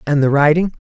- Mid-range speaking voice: Yes, medium, 150 Hz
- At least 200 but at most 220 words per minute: Yes, fast, 215 wpm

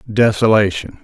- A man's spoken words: Yes, male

